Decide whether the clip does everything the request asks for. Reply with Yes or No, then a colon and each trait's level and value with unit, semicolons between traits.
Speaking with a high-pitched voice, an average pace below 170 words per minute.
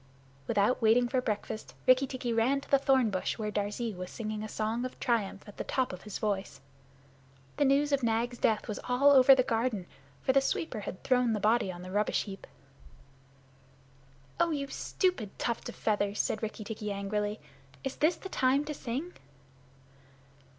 No: high, 230 Hz; average, 180 wpm